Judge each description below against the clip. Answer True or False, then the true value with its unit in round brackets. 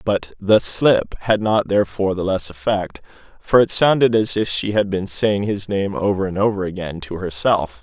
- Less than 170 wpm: False (200 wpm)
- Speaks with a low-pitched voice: True (100 Hz)